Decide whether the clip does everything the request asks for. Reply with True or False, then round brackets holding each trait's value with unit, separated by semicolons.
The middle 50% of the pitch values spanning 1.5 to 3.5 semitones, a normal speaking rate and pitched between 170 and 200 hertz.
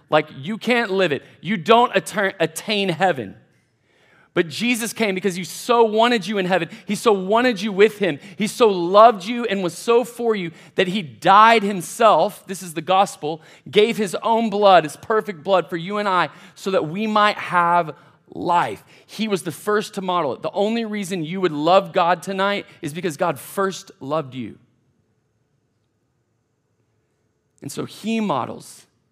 False (4.6 semitones; 175 wpm; 190 Hz)